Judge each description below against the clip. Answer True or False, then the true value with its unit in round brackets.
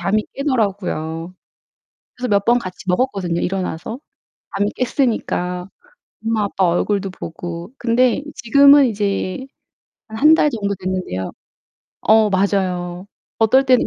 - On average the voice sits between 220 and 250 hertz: False (200 Hz)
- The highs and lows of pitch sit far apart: False (4.7 semitones)